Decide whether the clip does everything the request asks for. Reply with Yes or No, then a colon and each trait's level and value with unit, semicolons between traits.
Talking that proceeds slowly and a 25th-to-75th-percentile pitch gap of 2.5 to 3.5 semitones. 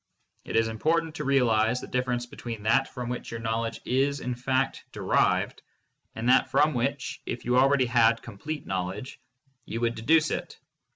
No: average, 170 wpm; average, 2.8 semitones